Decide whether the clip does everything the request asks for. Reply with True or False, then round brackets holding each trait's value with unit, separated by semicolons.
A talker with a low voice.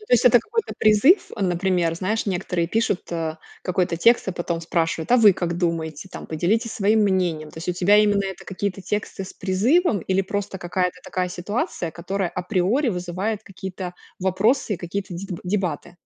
False (190 Hz)